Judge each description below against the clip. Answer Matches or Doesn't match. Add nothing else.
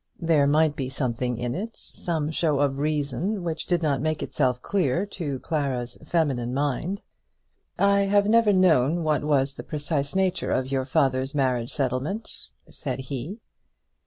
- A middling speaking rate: Matches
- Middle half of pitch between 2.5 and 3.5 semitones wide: Doesn't match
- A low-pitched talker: Doesn't match